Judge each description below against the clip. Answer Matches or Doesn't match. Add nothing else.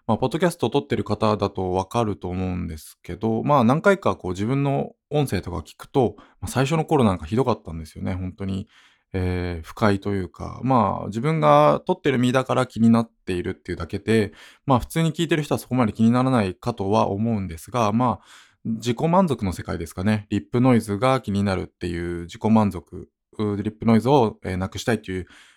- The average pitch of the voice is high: Doesn't match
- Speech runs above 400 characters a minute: Matches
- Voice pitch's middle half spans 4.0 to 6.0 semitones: Matches